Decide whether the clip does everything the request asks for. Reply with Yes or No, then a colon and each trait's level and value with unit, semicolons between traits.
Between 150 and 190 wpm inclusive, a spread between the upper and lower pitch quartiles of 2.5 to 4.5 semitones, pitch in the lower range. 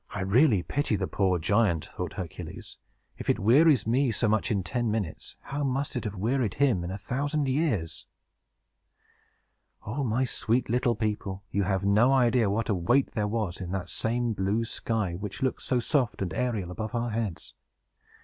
Yes: average, 180 wpm; average, 4.2 semitones; low, 110 Hz